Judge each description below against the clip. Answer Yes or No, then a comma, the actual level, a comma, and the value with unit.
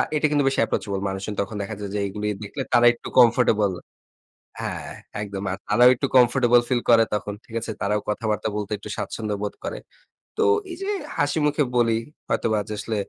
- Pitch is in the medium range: No, low, 110 Hz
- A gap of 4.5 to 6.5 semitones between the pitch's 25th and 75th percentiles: No, average, 2.8 semitones